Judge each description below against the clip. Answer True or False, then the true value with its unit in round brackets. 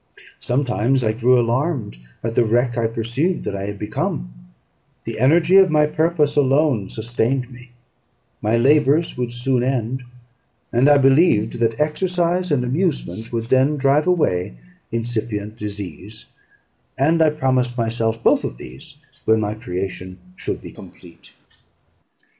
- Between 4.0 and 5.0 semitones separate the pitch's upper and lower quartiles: True (4.7 semitones)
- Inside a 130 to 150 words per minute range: True (140 wpm)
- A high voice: False (125 Hz)